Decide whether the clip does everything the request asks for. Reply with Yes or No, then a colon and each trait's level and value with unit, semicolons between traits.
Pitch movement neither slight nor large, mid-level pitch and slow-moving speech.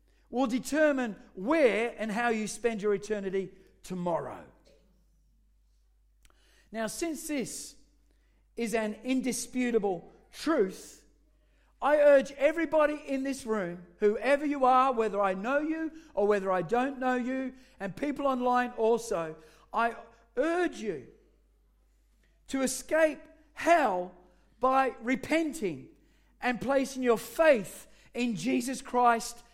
No: average, 4.5 semitones; high, 245 Hz; slow, 110 wpm